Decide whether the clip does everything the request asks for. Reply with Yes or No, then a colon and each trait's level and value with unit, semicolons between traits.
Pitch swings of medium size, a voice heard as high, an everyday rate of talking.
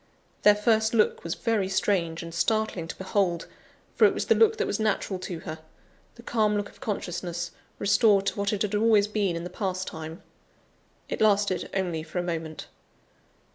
Yes: average, 3.5 semitones; high, 195 Hz; average, 185 wpm